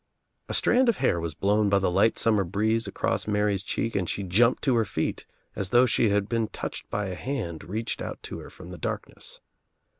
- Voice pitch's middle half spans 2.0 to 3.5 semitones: Yes, average, 2.9 semitones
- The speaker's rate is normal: No, fast, 215 wpm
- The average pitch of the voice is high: No, low, 105 Hz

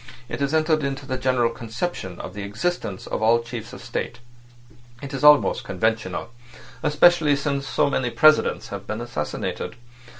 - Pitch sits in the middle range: No, low, 125 Hz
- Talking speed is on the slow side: No, average, 145 wpm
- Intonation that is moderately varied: Yes, average, 4.1 semitones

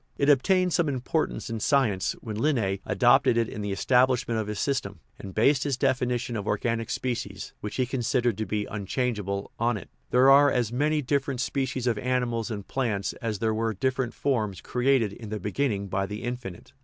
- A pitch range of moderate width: Yes, average, 3.9 semitones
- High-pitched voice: No, low, 120 Hz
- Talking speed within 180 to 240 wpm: Yes, average, 195 wpm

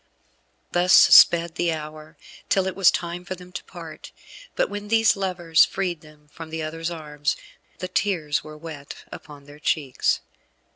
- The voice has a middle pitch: Yes, medium, 165 Hz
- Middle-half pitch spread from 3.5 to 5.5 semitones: No, average, 2.9 semitones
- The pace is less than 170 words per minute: Yes, average, 160 wpm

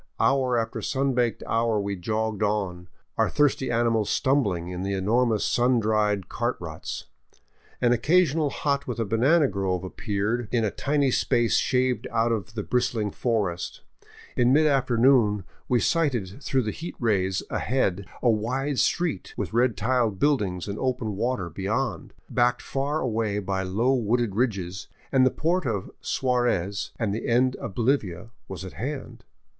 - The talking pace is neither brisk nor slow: Yes, average, 160 wpm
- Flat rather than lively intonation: No, average, 4.3 semitones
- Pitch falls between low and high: No, low, 115 Hz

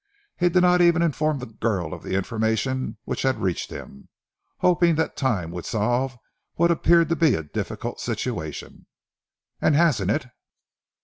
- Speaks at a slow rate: No, average, 160 wpm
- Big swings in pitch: Yes, wide, 8.0 semitones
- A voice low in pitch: Yes, low, 130 Hz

